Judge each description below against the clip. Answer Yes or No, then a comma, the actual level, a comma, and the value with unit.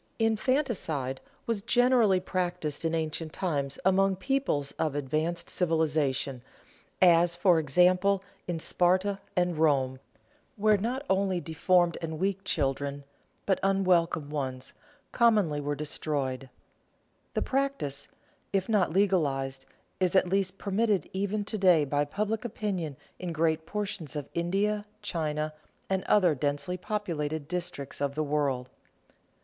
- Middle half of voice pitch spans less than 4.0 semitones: No, average, 4.8 semitones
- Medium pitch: Yes, medium, 175 Hz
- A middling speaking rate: No, slow, 125 wpm